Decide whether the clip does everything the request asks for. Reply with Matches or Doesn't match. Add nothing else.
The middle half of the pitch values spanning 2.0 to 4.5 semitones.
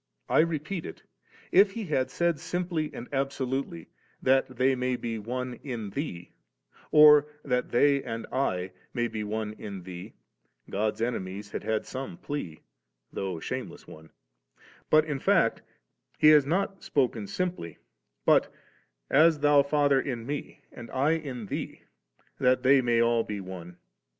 Doesn't match